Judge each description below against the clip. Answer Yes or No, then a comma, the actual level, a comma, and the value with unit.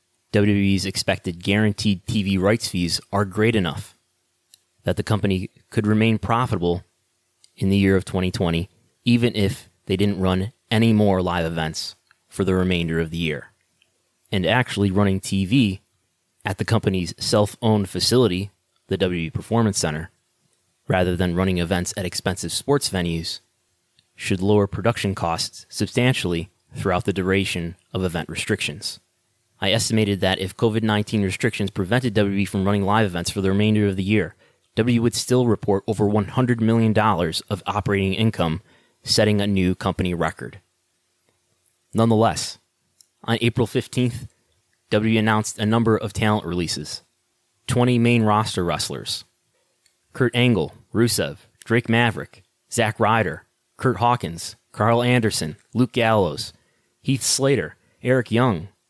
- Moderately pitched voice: No, low, 105 Hz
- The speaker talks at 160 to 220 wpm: No, slow, 135 wpm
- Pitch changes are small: No, average, 3.9 semitones